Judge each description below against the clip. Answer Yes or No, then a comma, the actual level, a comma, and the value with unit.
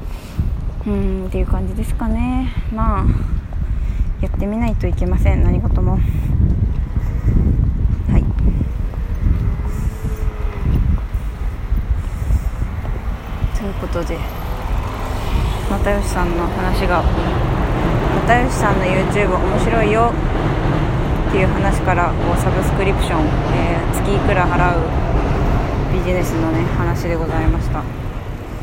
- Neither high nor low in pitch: No, very low, 90 Hz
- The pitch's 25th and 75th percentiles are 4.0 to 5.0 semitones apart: No, average, 3.4 semitones